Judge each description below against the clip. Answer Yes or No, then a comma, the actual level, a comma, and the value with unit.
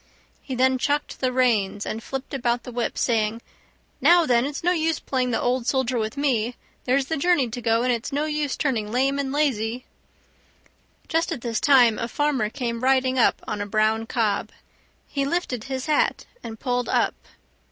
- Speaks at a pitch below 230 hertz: No, very high, 255 Hz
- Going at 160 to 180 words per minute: No, average, 190 wpm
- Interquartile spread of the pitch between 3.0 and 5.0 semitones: Yes, average, 3.3 semitones